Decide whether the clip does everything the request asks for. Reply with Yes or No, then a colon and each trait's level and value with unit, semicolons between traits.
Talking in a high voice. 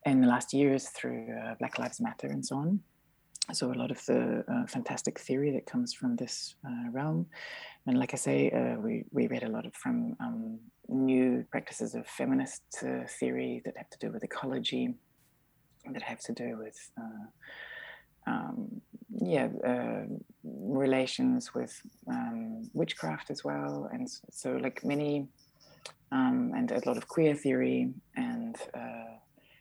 No: medium, 165 Hz